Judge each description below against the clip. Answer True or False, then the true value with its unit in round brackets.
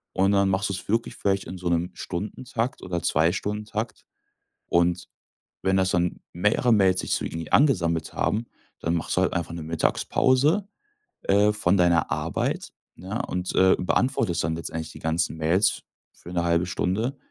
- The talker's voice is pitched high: False (95 Hz)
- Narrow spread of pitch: False (3.5 semitones)